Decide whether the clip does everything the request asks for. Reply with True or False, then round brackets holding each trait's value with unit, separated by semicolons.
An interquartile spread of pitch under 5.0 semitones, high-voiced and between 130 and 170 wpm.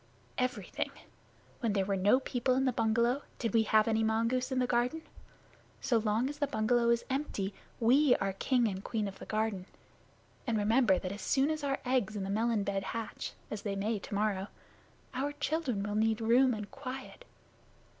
False (3.6 semitones; 230 Hz; 185 wpm)